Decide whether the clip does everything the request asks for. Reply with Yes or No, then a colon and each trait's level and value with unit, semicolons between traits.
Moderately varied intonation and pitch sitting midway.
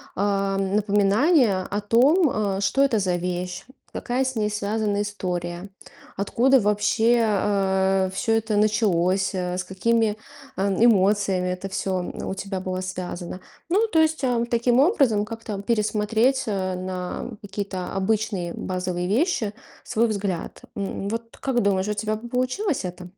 No: average, 3.4 semitones; high, 205 Hz